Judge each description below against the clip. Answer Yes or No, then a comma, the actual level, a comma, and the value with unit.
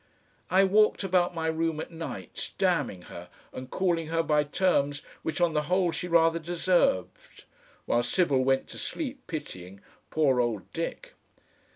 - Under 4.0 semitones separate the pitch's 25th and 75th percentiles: No, average, 4.9 semitones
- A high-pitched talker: No, medium, 160 Hz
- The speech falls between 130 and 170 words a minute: Yes, average, 155 wpm